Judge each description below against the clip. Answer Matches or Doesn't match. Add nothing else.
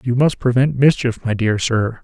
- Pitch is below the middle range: Matches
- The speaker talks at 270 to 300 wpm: Doesn't match